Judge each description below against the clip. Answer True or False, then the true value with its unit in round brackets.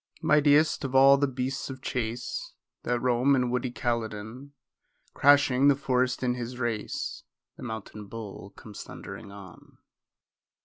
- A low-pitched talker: True (125 Hz)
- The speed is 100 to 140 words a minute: True (135 wpm)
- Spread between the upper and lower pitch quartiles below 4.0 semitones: True (3.1 semitones)